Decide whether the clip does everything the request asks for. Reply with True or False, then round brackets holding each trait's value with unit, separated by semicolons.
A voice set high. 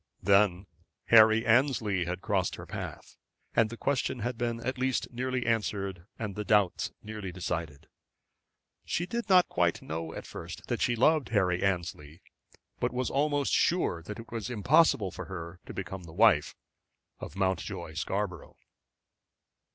False (105 Hz)